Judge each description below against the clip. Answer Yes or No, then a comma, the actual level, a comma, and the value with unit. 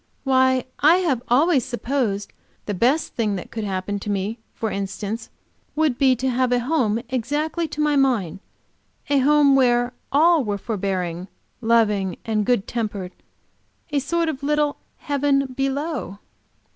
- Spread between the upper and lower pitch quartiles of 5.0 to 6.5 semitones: Yes, wide, 5.4 semitones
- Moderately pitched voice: No, very high, 250 Hz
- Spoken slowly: No, average, 145 wpm